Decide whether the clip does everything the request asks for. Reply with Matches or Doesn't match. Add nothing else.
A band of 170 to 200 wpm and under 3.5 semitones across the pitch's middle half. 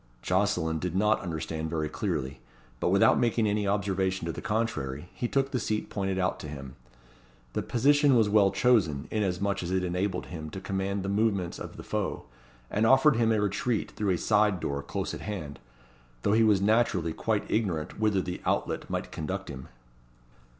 Doesn't match